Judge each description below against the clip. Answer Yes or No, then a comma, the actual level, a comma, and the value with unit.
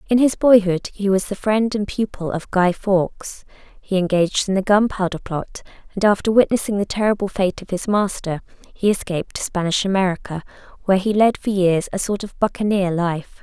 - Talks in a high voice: Yes, high, 195 Hz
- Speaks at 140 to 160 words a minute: No, average, 190 wpm